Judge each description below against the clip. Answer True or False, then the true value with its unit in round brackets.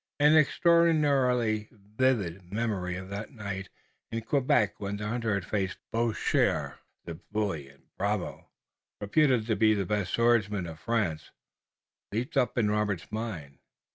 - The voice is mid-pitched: False (105 Hz)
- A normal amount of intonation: True (3.4 semitones)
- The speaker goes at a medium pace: False (130 wpm)